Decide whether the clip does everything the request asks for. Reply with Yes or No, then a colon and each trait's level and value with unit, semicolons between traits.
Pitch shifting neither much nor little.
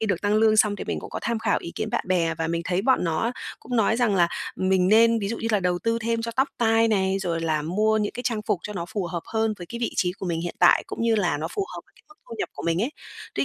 Yes: average, 4.3 semitones